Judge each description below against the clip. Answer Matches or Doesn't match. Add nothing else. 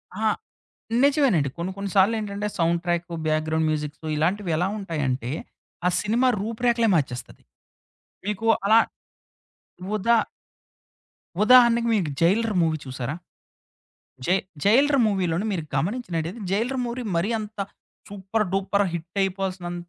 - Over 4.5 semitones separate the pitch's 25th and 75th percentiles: Matches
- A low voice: Doesn't match